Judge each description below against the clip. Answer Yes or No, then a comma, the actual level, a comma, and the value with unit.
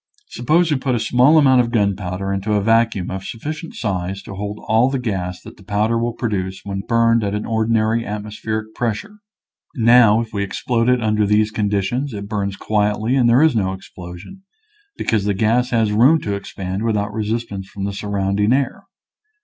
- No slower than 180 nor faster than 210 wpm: Yes, average, 185 wpm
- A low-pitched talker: Yes, low, 110 Hz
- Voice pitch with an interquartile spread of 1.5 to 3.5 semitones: Yes, average, 2.8 semitones